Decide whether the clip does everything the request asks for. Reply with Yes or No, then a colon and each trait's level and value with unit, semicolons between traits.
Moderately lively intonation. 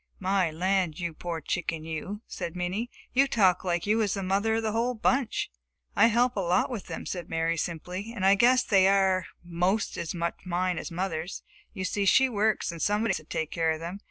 Yes: average, 3.7 semitones